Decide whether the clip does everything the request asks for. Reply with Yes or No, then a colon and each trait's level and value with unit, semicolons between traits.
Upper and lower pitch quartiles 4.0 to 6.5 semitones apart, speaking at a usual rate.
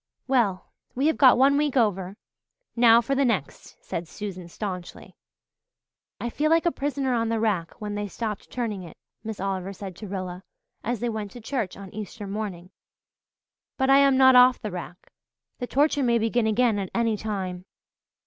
Yes: average, 4.5 semitones; average, 180 wpm